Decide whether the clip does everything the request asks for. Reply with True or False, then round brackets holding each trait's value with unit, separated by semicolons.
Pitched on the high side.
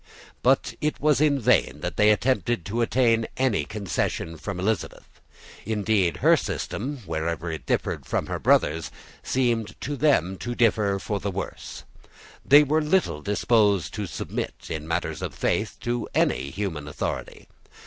False (105 Hz)